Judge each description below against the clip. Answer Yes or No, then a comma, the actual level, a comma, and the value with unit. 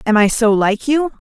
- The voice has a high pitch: Yes, high, 235 Hz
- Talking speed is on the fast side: Yes, fast, 235 wpm